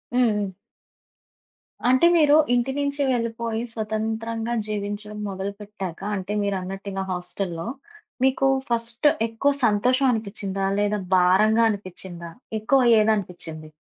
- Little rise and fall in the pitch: No, average, 3.1 semitones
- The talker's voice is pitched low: No, high, 210 Hz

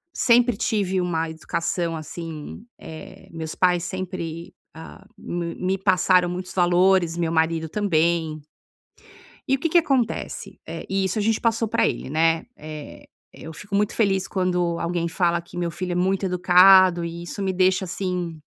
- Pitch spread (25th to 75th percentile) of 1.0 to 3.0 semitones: Yes, narrow, 2.4 semitones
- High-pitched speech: No, medium, 180 Hz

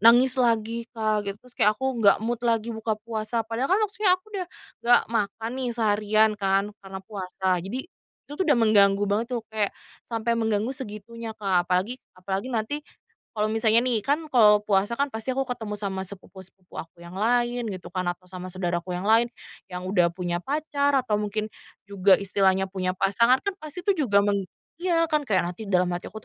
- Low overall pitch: No, high, 215 Hz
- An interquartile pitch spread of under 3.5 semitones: No, average, 3.8 semitones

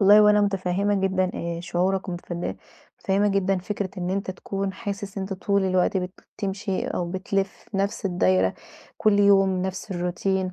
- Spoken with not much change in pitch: Yes, narrow, 1.5 semitones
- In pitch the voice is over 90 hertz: Yes, high, 190 Hz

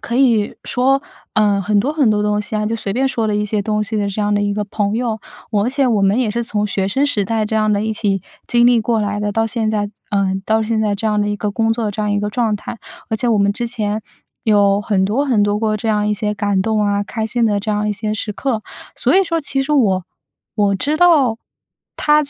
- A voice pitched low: No, high, 215 Hz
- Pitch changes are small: Yes, narrow, 2.1 semitones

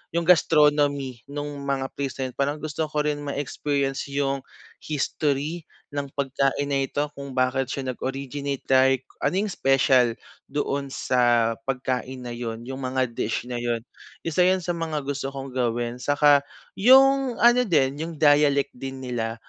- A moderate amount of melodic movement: No, narrow, 2.1 semitones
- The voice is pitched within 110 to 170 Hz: Yes, medium, 140 Hz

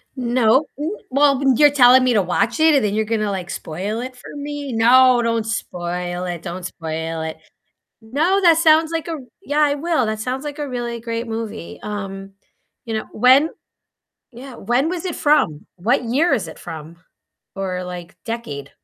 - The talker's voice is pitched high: Yes, high, 235 Hz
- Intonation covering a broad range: Yes, wide, 6.7 semitones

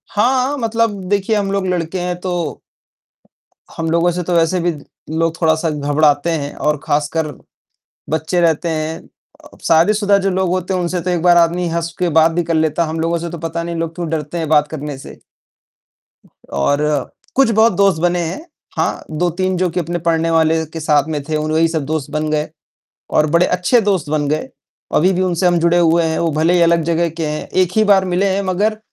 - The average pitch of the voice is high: No, medium, 170 Hz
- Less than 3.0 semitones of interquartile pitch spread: Yes, narrow, 2.4 semitones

